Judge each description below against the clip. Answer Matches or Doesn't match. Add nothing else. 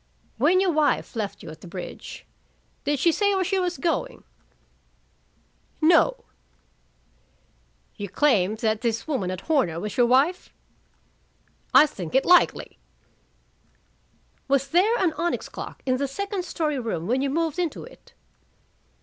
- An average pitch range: Doesn't match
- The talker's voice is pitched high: Matches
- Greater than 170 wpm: Doesn't match